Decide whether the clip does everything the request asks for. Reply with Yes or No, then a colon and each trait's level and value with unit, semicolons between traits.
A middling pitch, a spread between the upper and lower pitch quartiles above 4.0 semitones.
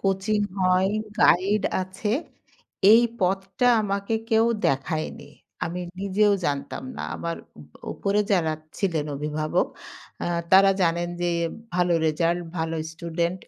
No: medium, 180 Hz; average, 3.1 semitones